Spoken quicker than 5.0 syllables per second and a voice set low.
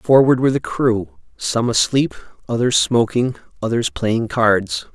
No: 4.3 syllables/s; low, 120 Hz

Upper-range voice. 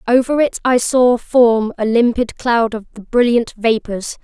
Yes: high, 235 Hz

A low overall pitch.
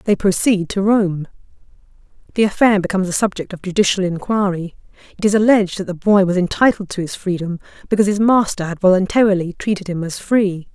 No: high, 190 Hz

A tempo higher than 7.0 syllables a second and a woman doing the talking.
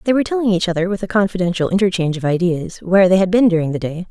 Yes: 7.7 syllables/s; female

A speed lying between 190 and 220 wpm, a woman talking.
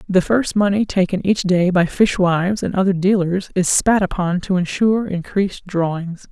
No: average, 170 wpm; female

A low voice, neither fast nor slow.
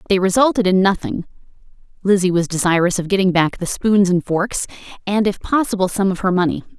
No: high, 190 Hz; average, 185 wpm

